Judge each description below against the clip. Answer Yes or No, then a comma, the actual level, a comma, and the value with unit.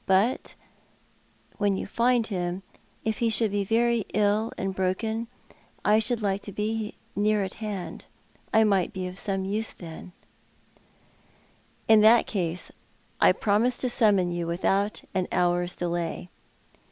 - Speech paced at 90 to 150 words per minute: Yes, average, 145 wpm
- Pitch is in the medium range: No, high, 205 Hz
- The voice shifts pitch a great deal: No, average, 3.1 semitones